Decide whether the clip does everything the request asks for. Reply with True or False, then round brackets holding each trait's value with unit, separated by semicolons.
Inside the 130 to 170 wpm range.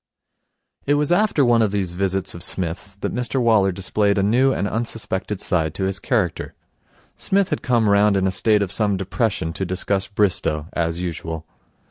False (180 wpm)